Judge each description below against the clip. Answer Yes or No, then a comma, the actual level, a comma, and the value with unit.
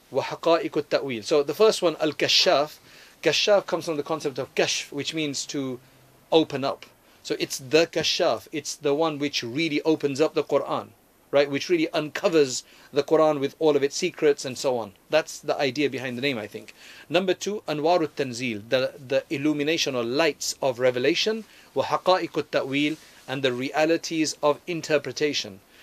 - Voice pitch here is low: No, medium, 150 Hz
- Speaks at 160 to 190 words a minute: Yes, average, 165 wpm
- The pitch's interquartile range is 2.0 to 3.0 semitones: Yes, average, 2.7 semitones